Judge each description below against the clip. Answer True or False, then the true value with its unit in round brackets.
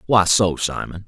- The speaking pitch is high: False (95 Hz)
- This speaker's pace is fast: False (165 wpm)